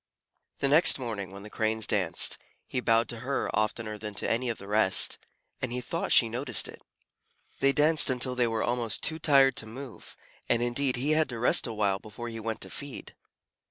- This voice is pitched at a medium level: No, low, 120 Hz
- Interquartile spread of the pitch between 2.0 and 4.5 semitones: Yes, average, 3.3 semitones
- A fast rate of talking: Yes, fast, 210 wpm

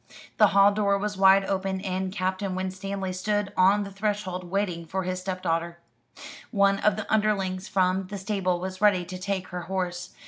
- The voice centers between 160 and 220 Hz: Yes, high, 190 Hz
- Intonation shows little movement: Yes, narrow, 1.4 semitones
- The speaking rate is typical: Yes, average, 175 wpm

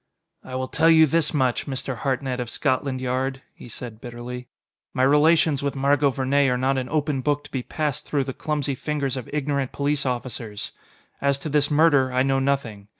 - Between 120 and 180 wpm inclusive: No, average, 195 wpm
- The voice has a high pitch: No, low, 135 Hz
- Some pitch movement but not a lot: No, narrow, 2.2 semitones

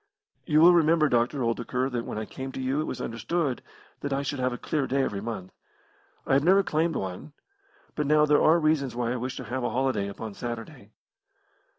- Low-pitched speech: Yes, low, 130 Hz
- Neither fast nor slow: No, fast, 215 wpm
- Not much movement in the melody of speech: No, average, 4.3 semitones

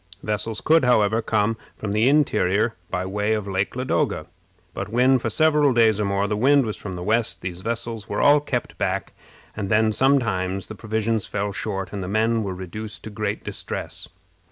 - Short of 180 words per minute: No, average, 190 wpm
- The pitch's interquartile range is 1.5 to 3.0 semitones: Yes, average, 2.7 semitones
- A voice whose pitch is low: Yes, low, 110 Hz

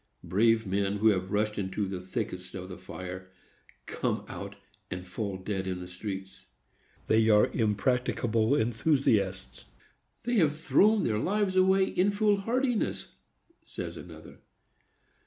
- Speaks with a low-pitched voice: Yes, low, 105 Hz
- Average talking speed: No, slow, 130 wpm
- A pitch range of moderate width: No, wide, 8.2 semitones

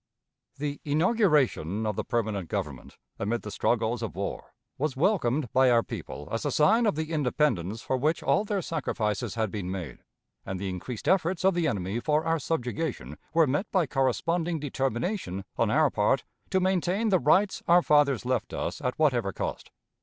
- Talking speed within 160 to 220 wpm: Yes, average, 175 wpm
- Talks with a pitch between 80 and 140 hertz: Yes, low, 135 Hz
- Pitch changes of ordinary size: No, wide, 7.1 semitones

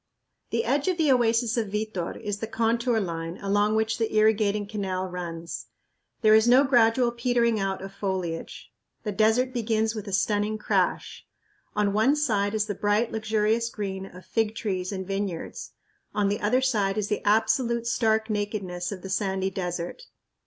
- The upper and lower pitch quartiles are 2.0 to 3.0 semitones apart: Yes, average, 2.7 semitones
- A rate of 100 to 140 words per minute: No, average, 170 wpm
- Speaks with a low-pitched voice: No, high, 215 Hz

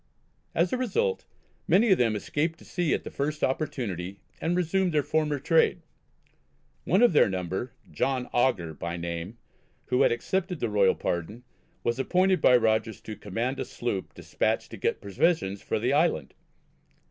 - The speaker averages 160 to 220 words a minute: Yes, average, 165 wpm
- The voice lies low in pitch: Yes, low, 130 Hz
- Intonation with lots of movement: Yes, wide, 8.6 semitones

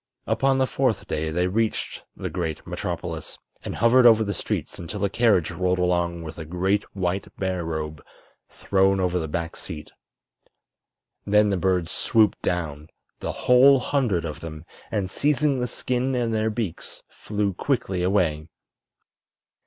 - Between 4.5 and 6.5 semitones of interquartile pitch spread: Yes, average, 4.8 semitones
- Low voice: Yes, very low, 95 Hz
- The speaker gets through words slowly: No, average, 145 wpm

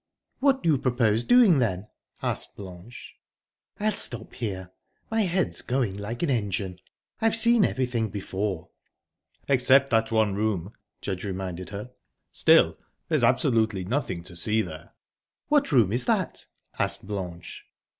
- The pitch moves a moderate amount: No, wide, 5.7 semitones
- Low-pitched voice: Yes, low, 110 Hz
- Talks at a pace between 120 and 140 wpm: Yes, slow, 135 wpm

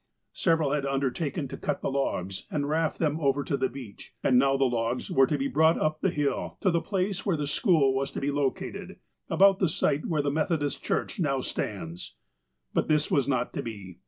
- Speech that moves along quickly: Yes, fast, 215 wpm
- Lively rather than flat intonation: No, average, 3.2 semitones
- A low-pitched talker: No, medium, 145 Hz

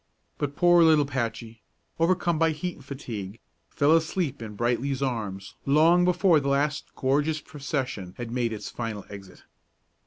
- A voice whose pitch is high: No, medium, 140 Hz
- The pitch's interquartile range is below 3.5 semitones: No, wide, 5.5 semitones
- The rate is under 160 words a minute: Yes, average, 150 wpm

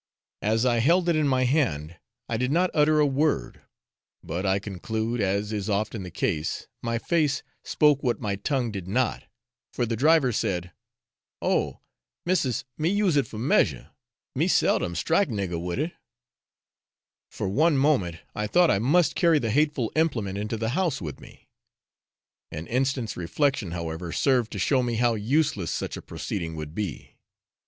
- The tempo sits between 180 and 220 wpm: No, average, 165 wpm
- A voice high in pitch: No, low, 115 Hz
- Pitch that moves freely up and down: Yes, wide, 6.9 semitones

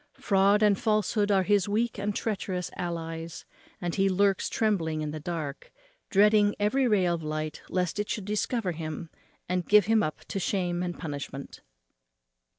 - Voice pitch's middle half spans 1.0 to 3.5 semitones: No, average, 3.9 semitones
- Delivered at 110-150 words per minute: No, average, 160 wpm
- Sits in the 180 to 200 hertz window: Yes, high, 190 Hz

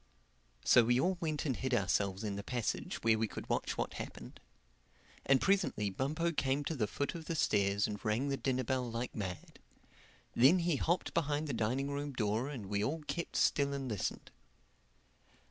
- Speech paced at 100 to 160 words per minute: No, average, 185 wpm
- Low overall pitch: Yes, low, 130 Hz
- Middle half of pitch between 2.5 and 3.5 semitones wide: No, average, 5.2 semitones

